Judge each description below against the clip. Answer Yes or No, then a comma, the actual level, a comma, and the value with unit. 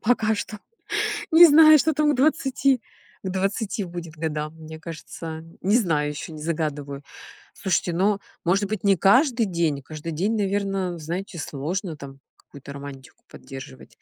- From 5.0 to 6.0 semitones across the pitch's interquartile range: Yes, wide, 5.6 semitones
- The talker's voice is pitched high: No, medium, 175 Hz